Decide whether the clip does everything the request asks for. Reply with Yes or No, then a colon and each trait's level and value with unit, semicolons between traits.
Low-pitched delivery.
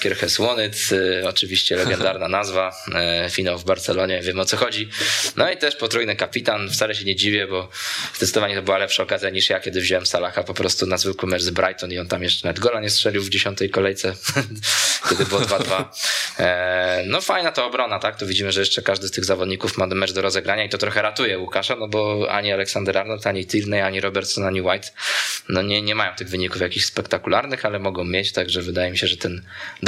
Yes: very low, 95 Hz